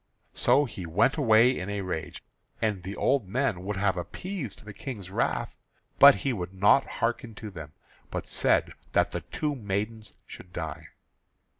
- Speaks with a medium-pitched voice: No, low, 105 Hz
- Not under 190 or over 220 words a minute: No, average, 165 wpm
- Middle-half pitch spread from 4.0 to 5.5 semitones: Yes, average, 5.0 semitones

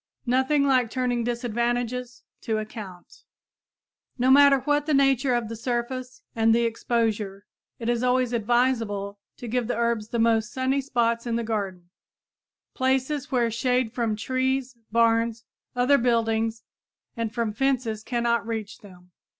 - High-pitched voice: Yes, high, 235 Hz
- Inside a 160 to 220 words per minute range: No, average, 140 wpm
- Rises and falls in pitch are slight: Yes, narrow, 2.2 semitones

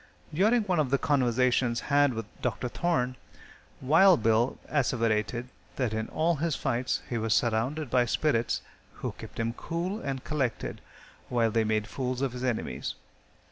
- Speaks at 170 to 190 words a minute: No, average, 155 wpm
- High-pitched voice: No, low, 125 Hz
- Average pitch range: Yes, average, 4.4 semitones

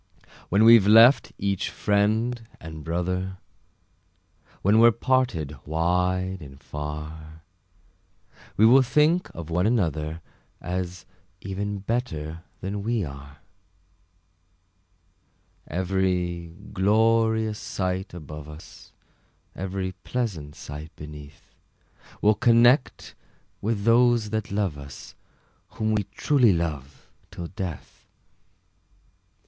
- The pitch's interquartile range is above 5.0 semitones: Yes, wide, 5.6 semitones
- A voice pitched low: Yes, very low, 95 Hz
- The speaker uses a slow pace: Yes, slow, 95 wpm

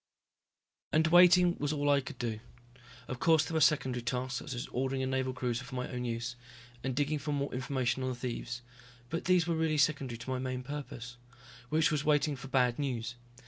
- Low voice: Yes, low, 130 Hz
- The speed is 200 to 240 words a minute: Yes, fast, 205 wpm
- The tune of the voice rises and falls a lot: No, average, 3.2 semitones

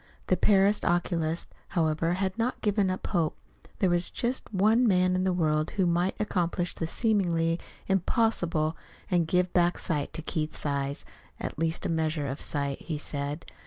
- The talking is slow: No, average, 165 wpm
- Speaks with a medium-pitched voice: Yes, medium, 175 Hz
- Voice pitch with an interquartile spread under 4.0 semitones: Yes, average, 3.2 semitones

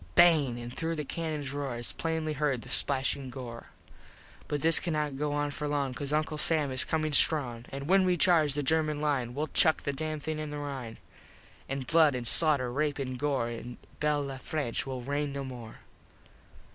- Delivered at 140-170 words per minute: No, average, 200 wpm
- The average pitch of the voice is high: No, medium, 145 Hz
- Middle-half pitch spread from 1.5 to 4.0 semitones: Yes, average, 2.7 semitones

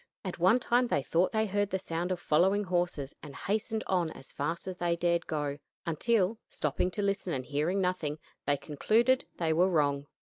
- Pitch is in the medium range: Yes, medium, 175 Hz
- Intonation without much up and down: No, average, 4.6 semitones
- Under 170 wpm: No, average, 195 wpm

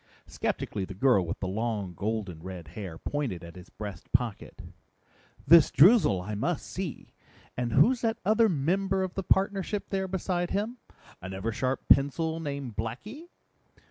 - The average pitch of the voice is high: No, low, 130 Hz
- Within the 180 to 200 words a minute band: No, average, 150 wpm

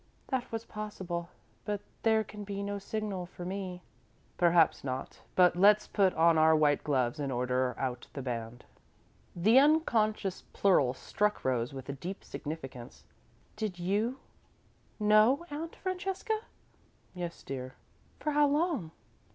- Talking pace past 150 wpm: No, slow, 135 wpm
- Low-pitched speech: No, medium, 185 Hz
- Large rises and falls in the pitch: Yes, wide, 7.0 semitones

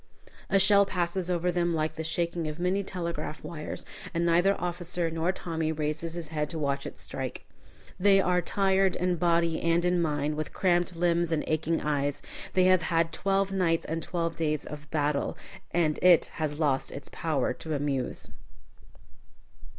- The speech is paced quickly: No, average, 170 wpm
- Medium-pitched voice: Yes, medium, 165 Hz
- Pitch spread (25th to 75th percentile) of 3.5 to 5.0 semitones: No, narrow, 2.4 semitones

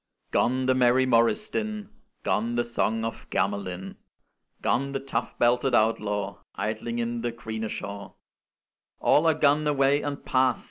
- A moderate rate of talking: Yes, average, 145 wpm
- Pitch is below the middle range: Yes, low, 120 Hz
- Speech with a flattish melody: No, average, 3.7 semitones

